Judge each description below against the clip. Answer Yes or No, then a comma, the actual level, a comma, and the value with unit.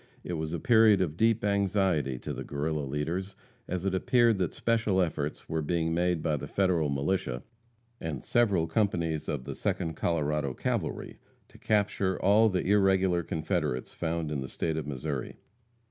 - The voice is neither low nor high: No, very low, 85 Hz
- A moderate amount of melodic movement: Yes, average, 4.3 semitones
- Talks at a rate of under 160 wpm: No, average, 165 wpm